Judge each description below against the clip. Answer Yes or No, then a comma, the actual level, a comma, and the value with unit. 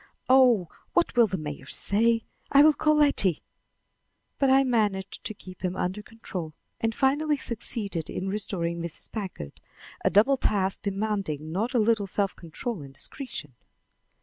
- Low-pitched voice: No, high, 205 Hz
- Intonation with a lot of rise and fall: No, average, 5.0 semitones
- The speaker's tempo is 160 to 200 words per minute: No, average, 150 wpm